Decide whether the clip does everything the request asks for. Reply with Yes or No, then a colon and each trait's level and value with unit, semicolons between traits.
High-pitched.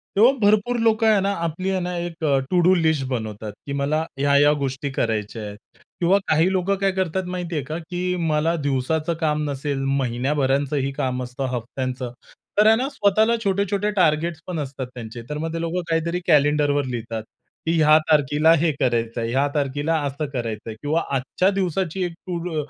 No: medium, 150 Hz